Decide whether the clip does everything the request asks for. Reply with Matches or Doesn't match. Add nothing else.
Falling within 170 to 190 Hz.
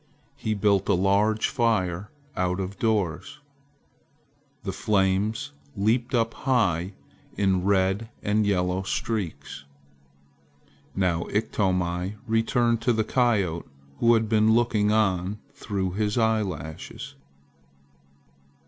Doesn't match